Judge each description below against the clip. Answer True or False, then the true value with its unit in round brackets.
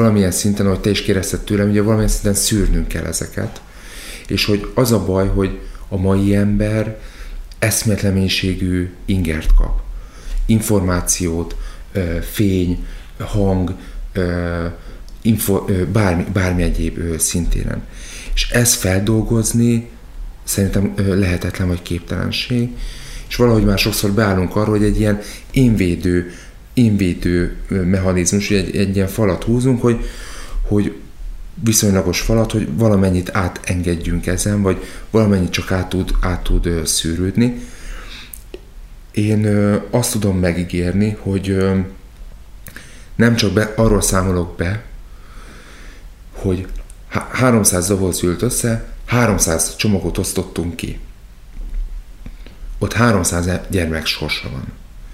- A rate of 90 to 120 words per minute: True (105 wpm)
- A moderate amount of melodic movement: True (3.2 semitones)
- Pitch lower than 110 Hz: True (95 Hz)